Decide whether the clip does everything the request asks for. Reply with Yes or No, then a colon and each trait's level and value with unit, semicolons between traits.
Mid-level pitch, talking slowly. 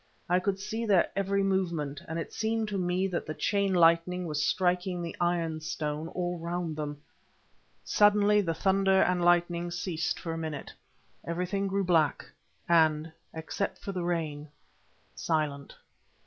No: medium, 175 Hz; average, 150 wpm